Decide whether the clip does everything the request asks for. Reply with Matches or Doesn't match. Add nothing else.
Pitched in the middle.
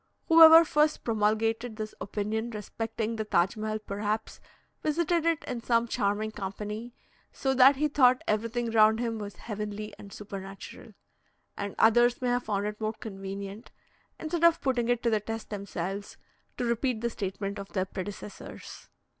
Doesn't match